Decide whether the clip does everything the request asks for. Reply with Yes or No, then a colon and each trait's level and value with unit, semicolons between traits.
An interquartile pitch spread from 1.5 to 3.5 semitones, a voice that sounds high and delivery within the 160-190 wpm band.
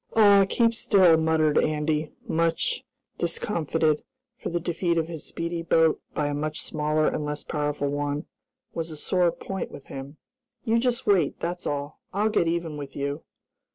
No: average, 2.8 semitones; medium, 160 Hz; average, 165 wpm